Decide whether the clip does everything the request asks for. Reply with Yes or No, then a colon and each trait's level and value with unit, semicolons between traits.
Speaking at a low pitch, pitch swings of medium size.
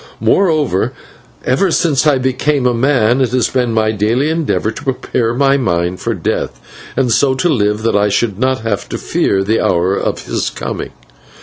Yes: low, 125 Hz; average, 4.2 semitones